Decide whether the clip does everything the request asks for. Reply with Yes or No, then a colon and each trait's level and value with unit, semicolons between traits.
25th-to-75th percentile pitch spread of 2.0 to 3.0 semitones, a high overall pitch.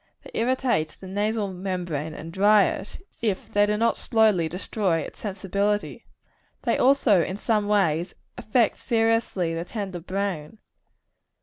No: average, 3.5 semitones; high, 200 Hz